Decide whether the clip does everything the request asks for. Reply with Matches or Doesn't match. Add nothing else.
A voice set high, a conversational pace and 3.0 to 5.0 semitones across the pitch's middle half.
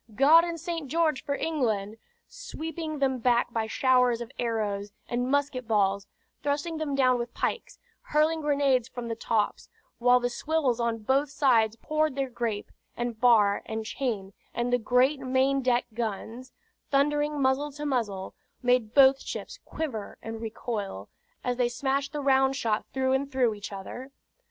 Matches